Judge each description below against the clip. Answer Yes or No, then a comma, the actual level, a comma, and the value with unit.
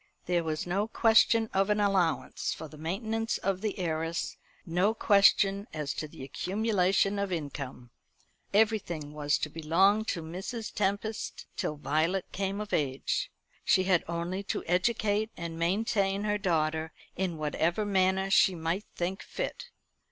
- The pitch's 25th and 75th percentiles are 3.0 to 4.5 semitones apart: Yes, average, 4.1 semitones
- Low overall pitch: No, medium, 185 Hz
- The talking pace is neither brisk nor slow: Yes, average, 145 wpm